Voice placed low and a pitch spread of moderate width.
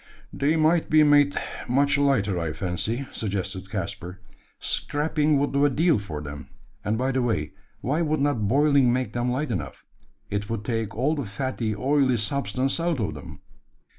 No: low, 130 Hz; wide, 5.9 semitones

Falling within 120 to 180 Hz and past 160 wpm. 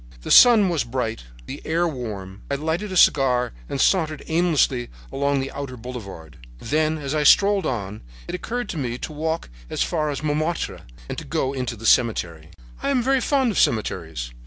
Yes: medium, 140 Hz; average, 180 wpm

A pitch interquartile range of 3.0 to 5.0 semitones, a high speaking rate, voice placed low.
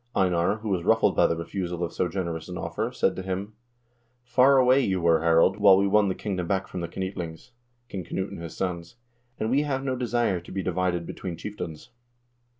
Yes: average, 3.6 semitones; fast, 210 wpm; very low, 95 Hz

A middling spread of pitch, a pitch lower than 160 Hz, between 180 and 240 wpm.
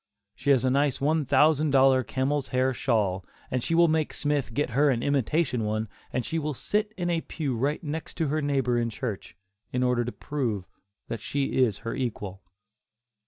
Yes: average, 3.7 semitones; low, 135 Hz; average, 195 wpm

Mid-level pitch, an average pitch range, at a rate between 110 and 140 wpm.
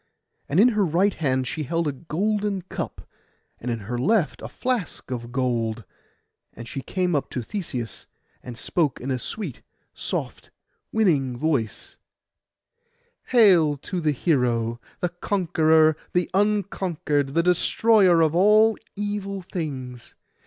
No: medium, 160 Hz; wide, 7.1 semitones; slow, 135 wpm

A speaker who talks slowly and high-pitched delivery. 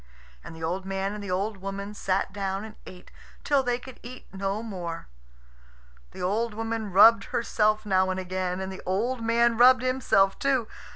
No: average, 180 wpm; high, 205 Hz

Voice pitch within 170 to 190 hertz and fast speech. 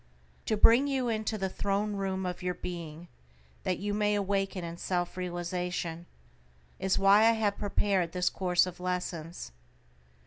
No: medium, 185 Hz; average, 150 wpm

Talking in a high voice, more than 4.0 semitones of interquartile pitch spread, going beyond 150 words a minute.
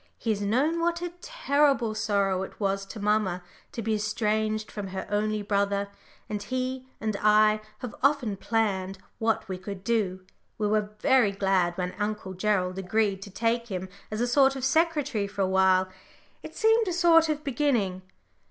Yes: high, 215 Hz; average, 4.5 semitones; average, 175 wpm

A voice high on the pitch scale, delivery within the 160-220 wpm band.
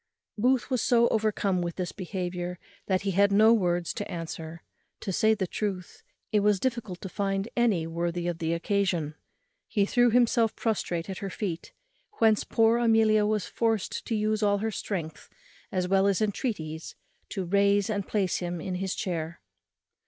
Yes: high, 200 Hz; average, 170 wpm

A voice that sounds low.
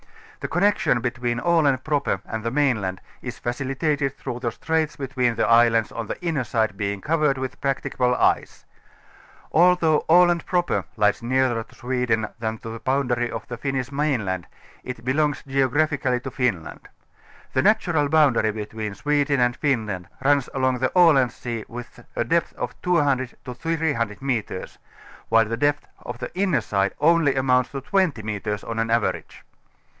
Yes: low, 130 Hz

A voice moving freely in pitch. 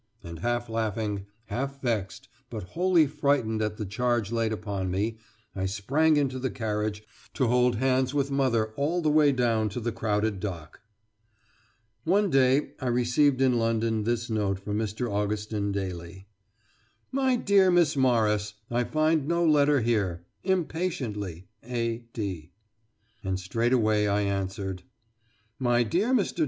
No: average, 4.8 semitones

